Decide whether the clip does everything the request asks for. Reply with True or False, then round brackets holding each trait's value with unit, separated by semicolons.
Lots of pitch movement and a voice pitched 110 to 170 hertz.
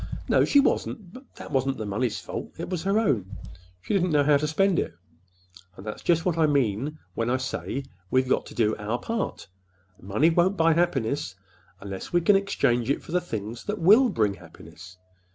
True (8.8 semitones; 140 Hz)